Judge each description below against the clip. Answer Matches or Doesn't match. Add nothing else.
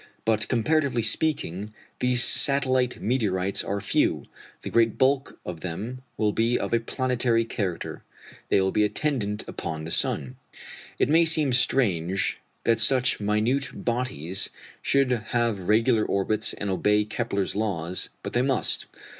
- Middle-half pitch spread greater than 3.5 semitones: Matches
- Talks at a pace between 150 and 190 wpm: Doesn't match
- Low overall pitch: Matches